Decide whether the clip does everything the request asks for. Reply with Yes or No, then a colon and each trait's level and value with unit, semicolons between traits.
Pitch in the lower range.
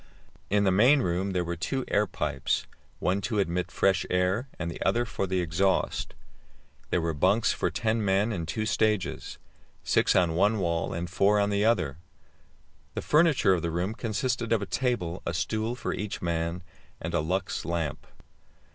Yes: very low, 95 Hz